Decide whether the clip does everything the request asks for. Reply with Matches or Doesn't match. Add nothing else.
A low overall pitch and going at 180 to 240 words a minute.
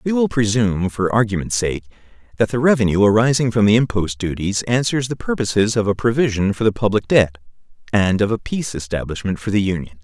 Matches